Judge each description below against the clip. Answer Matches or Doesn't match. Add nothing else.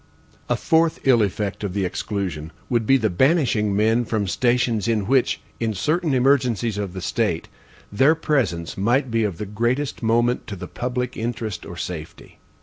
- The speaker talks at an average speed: Matches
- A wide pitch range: Doesn't match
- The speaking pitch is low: Matches